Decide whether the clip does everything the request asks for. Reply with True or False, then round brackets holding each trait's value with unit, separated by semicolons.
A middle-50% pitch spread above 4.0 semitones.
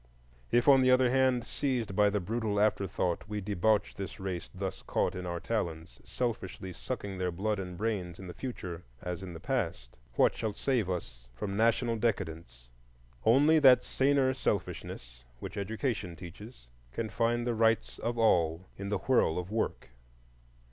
True (4.8 semitones)